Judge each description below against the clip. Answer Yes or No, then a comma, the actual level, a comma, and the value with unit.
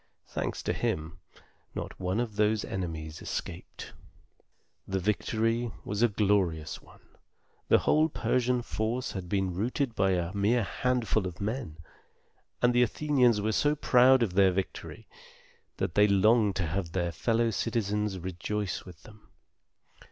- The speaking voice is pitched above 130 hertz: No, low, 105 Hz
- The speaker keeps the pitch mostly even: No, average, 4.1 semitones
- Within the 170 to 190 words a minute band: No, average, 145 wpm